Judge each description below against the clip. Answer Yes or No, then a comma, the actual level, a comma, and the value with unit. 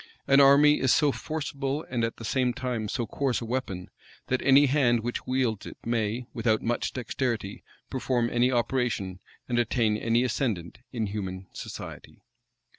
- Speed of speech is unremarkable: Yes, average, 160 wpm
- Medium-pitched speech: No, low, 120 Hz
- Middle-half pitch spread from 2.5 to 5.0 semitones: Yes, average, 2.9 semitones